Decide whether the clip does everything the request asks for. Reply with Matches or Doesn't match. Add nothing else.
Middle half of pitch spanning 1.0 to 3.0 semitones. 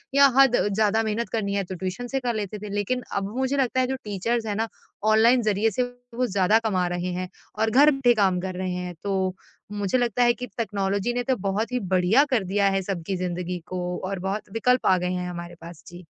Doesn't match